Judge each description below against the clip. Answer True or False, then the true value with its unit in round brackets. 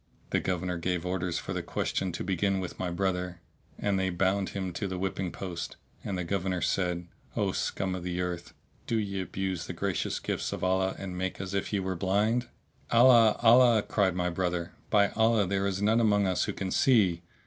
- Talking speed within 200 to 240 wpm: True (205 wpm)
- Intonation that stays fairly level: True (1.9 semitones)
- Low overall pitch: True (95 Hz)